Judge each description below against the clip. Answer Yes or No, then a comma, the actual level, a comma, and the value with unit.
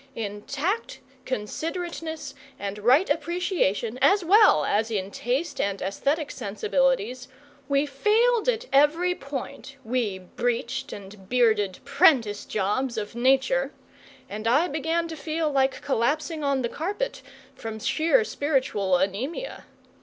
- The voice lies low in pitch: No, very high, 270 Hz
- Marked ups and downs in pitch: Yes, wide, 6.9 semitones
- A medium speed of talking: No, slow, 125 wpm